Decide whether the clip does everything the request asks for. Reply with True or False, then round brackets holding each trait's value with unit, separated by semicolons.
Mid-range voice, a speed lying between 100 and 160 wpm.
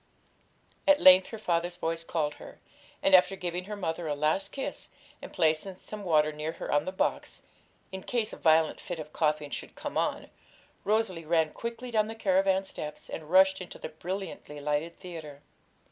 False (175 Hz; 180 wpm)